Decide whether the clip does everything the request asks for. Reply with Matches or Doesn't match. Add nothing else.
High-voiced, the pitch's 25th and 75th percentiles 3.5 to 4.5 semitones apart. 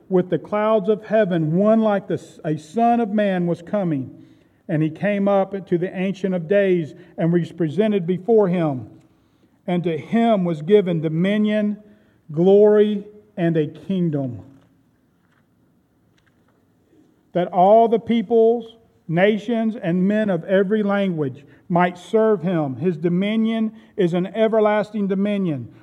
Matches